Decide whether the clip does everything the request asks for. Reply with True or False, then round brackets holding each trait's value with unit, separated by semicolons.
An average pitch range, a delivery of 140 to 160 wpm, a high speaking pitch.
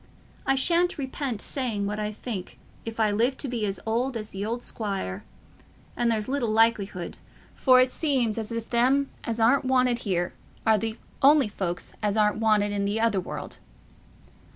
False (3.4 semitones; 175 wpm; 225 Hz)